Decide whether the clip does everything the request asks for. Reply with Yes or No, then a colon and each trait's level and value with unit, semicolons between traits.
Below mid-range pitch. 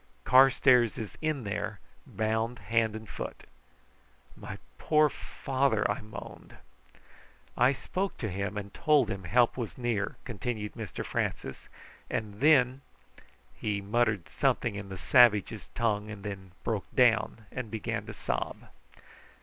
Yes: low, 110 Hz